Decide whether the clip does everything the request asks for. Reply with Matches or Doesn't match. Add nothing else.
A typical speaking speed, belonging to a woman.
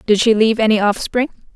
Matches